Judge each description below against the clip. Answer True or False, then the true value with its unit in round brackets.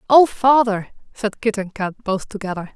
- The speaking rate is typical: True (175 wpm)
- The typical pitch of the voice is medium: False (215 Hz)